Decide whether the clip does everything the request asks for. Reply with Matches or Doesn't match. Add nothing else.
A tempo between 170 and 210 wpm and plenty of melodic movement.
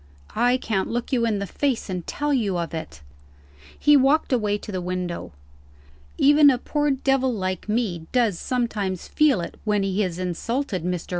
Matches